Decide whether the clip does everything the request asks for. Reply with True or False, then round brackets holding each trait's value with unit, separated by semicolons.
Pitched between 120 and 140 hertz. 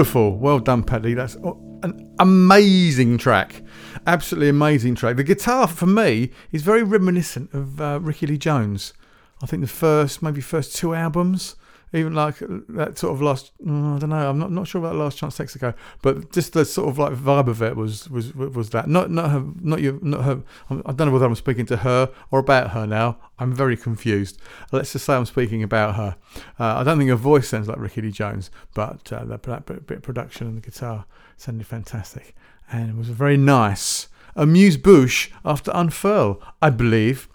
True (135 Hz)